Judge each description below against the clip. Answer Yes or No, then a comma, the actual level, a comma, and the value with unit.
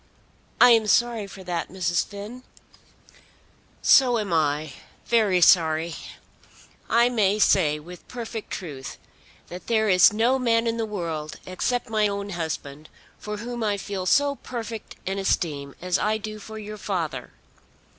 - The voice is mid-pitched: No, high, 200 Hz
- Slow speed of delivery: No, average, 145 wpm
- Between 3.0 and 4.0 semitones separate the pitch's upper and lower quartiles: No, average, 4.7 semitones